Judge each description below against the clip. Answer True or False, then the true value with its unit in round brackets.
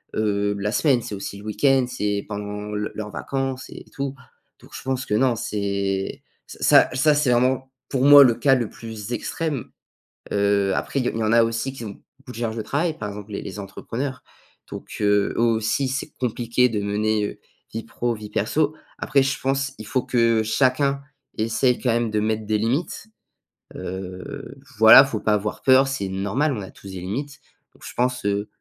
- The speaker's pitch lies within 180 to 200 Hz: False (115 Hz)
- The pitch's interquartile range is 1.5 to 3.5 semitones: False (4.2 semitones)